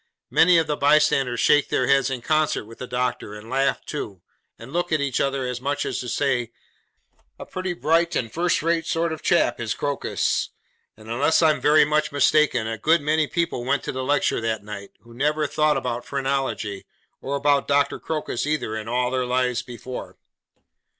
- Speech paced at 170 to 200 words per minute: Yes, average, 195 wpm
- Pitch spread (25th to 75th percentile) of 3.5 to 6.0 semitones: Yes, average, 3.9 semitones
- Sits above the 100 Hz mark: Yes, medium, 140 Hz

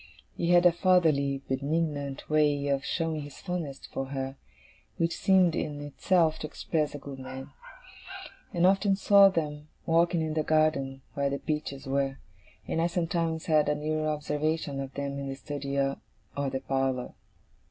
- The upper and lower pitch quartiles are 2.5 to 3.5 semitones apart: Yes, average, 3.0 semitones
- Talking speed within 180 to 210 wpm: No, average, 165 wpm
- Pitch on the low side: No, medium, 150 Hz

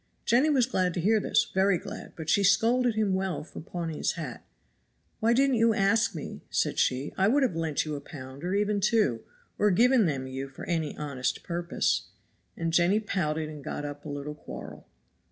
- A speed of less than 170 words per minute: No, average, 200 wpm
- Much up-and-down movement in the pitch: Yes, wide, 6.2 semitones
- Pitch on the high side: No, medium, 175 Hz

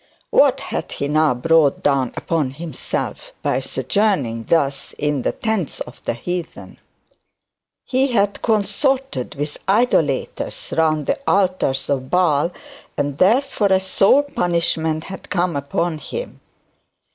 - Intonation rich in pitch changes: Yes, wide, 5.8 semitones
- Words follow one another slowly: Yes, slow, 125 wpm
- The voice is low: No, medium, 165 Hz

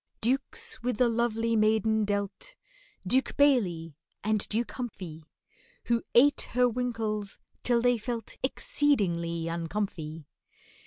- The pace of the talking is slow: Yes, slow, 110 wpm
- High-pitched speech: Yes, high, 220 Hz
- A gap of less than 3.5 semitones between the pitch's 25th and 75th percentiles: No, average, 4.1 semitones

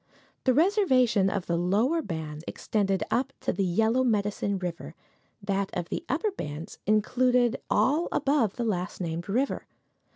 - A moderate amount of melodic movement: No, wide, 5.8 semitones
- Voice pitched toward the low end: No, high, 210 Hz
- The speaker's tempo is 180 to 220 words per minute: No, average, 150 wpm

